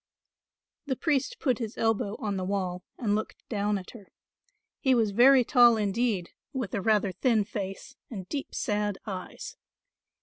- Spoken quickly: No, average, 160 wpm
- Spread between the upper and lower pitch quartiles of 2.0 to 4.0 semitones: Yes, average, 3.6 semitones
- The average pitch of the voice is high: Yes, high, 215 Hz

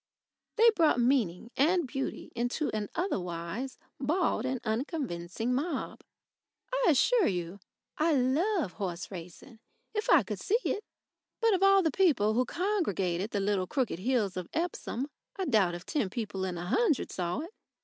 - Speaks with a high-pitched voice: Yes, very high, 250 Hz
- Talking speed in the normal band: Yes, average, 160 wpm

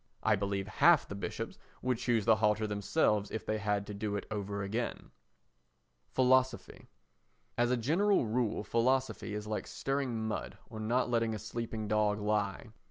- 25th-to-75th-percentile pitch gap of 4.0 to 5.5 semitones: No, average, 2.8 semitones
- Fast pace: No, average, 165 wpm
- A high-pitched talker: No, low, 110 Hz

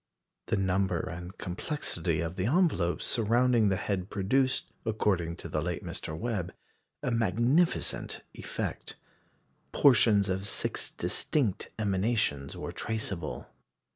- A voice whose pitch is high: No, low, 100 Hz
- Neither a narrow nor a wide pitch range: Yes, average, 4.8 semitones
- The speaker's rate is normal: No, slow, 115 wpm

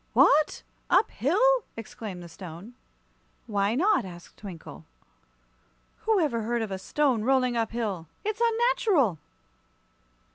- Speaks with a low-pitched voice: No, high, 235 Hz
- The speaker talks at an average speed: No, slow, 120 wpm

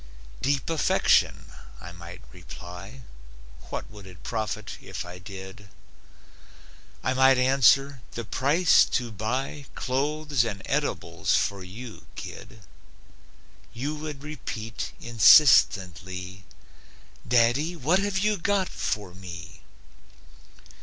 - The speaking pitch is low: Yes, low, 120 Hz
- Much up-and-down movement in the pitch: Yes, wide, 6.8 semitones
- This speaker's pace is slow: Yes, slow, 105 wpm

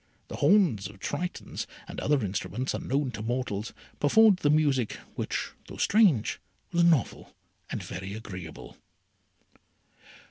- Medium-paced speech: No, slow, 120 wpm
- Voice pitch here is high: No, low, 130 Hz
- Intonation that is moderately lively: No, wide, 8.3 semitones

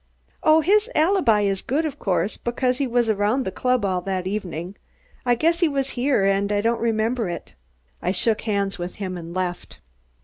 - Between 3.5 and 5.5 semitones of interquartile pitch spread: Yes, average, 5.0 semitones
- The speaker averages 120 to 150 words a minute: No, average, 195 wpm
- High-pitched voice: Yes, high, 215 Hz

